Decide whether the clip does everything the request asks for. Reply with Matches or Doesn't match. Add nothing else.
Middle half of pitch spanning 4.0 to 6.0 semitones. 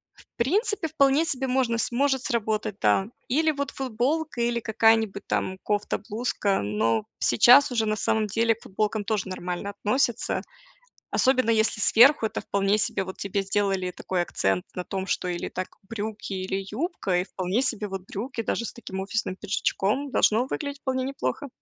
Matches